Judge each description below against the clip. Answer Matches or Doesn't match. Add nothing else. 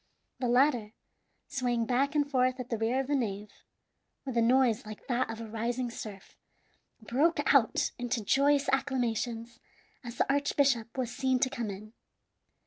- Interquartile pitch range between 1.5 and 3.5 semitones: Matches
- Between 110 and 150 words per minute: Doesn't match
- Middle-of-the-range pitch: Doesn't match